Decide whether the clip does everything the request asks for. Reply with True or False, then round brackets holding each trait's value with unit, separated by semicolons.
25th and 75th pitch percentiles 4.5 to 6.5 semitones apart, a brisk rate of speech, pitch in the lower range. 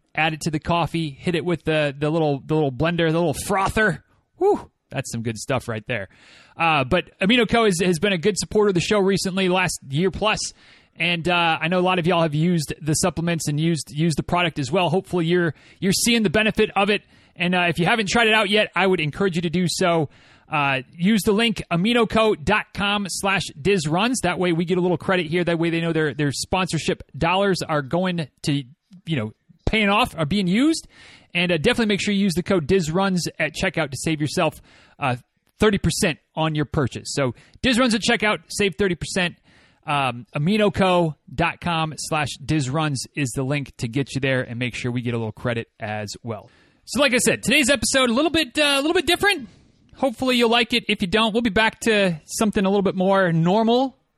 False (4.9 semitones; 215 wpm; 175 Hz)